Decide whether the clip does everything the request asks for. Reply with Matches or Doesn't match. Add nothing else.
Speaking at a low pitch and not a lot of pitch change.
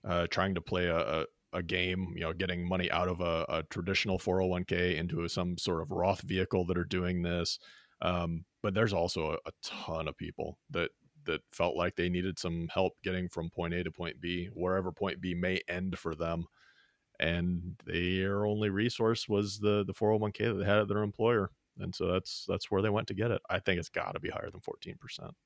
Matches